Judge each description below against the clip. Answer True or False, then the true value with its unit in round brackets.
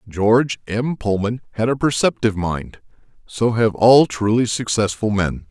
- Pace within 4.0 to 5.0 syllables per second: True (4.5 syllables/s)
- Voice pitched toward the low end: True (110 Hz)